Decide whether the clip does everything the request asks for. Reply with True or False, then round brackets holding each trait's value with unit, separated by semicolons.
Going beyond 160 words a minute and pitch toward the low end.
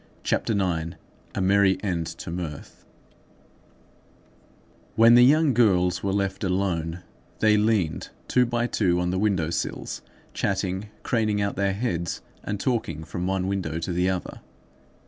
False (140 wpm; 95 Hz)